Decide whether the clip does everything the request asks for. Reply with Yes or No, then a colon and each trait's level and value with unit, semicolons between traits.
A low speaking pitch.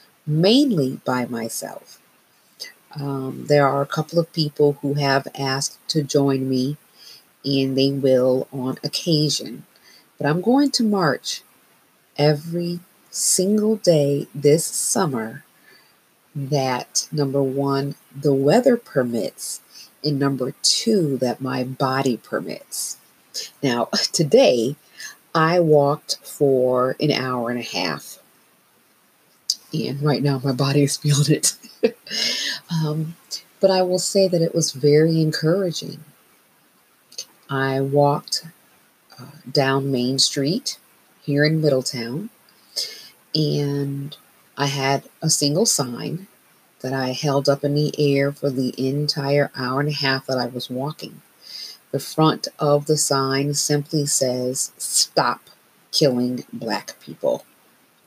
No: medium, 145 Hz